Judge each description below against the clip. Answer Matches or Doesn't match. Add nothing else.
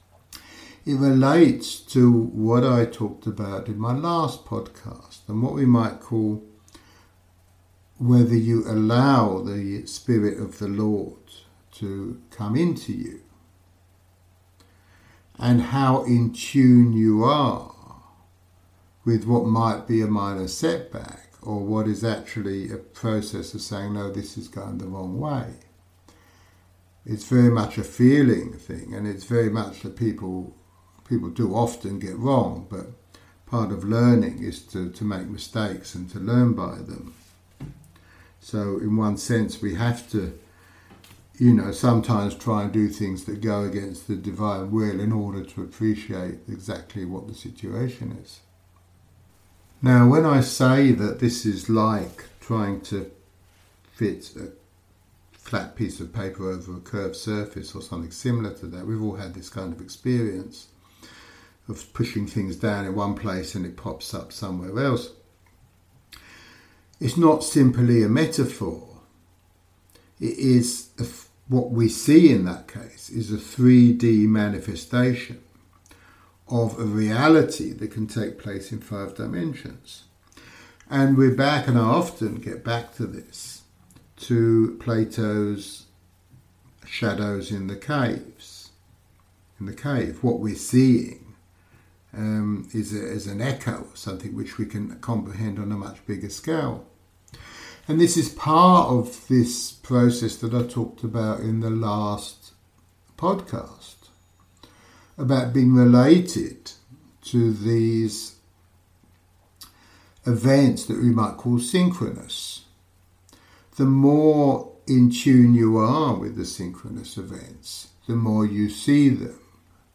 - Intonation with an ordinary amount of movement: Matches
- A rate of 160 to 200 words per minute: Doesn't match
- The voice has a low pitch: Matches